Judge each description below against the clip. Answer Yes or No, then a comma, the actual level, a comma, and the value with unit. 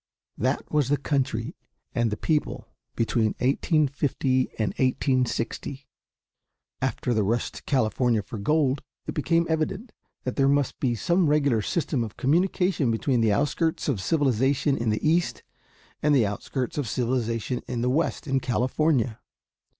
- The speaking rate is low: No, average, 145 wpm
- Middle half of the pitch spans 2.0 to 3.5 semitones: No, average, 4.2 semitones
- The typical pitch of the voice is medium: No, low, 130 Hz